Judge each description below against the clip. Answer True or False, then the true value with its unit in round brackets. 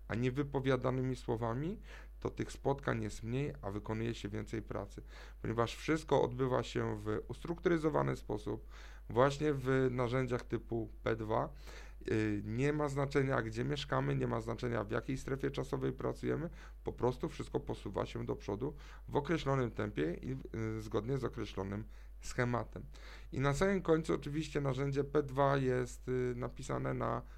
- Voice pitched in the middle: False (125 Hz)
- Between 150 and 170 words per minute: False (140 wpm)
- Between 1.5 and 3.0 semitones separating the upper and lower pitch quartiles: False (4.1 semitones)